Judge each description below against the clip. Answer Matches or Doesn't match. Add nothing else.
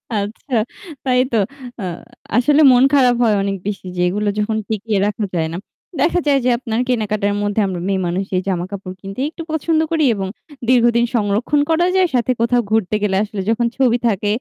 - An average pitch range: Matches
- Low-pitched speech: Doesn't match